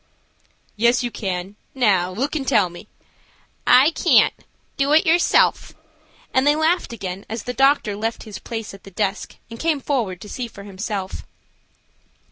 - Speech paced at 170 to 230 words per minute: No, average, 160 wpm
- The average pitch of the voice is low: No, high, 225 Hz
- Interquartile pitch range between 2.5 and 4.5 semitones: No, wide, 5.5 semitones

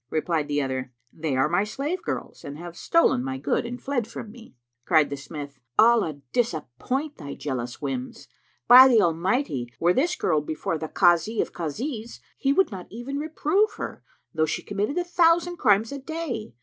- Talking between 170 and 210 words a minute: Yes, average, 180 wpm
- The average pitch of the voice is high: Yes, high, 195 Hz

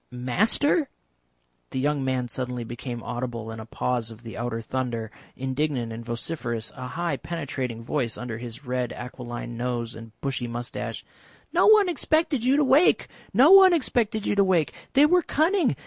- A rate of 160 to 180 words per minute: Yes, average, 165 wpm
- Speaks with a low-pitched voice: Yes, low, 130 Hz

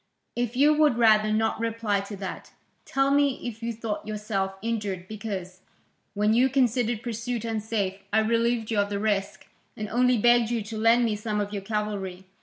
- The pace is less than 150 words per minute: No, average, 185 wpm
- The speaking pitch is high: Yes, high, 220 Hz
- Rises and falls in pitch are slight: Yes, narrow, 2.3 semitones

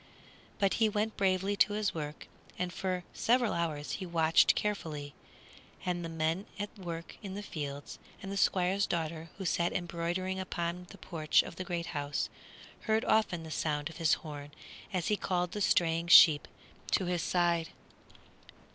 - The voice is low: No, medium, 175 Hz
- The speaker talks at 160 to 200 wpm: Yes, average, 165 wpm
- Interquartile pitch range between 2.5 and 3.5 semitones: Yes, average, 3.0 semitones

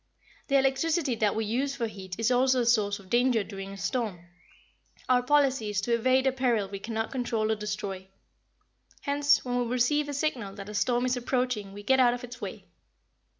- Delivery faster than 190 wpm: Yes, average, 200 wpm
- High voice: Yes, high, 240 Hz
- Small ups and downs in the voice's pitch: No, average, 3.9 semitones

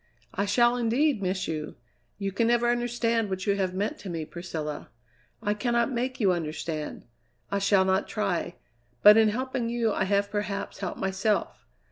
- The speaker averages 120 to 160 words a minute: No, average, 170 wpm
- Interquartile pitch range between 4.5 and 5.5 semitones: No, average, 3.8 semitones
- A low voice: No, high, 205 Hz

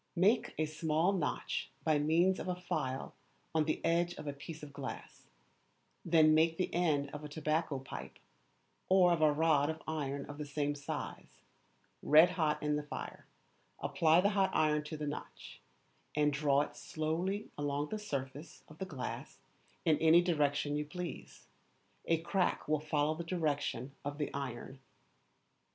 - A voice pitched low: No, medium, 155 Hz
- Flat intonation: Yes, narrow, 2.3 semitones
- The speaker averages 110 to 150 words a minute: No, average, 165 wpm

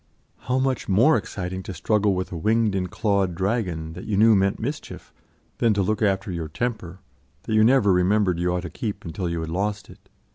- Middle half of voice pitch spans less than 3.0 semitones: No, average, 3.3 semitones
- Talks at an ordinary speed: No, fast, 210 wpm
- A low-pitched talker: Yes, low, 100 Hz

